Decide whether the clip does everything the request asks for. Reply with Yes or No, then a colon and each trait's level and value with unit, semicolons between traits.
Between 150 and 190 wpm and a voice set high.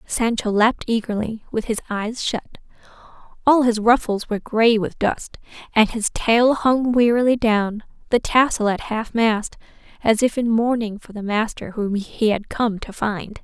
Yes: average, 170 wpm; high, 225 Hz